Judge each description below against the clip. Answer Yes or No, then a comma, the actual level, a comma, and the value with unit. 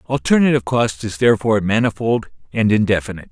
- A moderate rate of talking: No, slow, 125 wpm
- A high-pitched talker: No, low, 110 Hz